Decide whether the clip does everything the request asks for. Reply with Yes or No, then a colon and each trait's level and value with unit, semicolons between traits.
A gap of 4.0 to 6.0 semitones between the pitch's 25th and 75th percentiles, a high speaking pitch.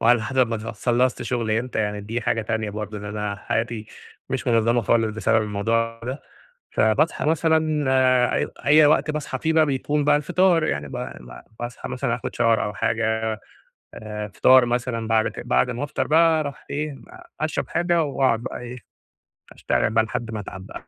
No: average, 4.7 semitones; low, 120 Hz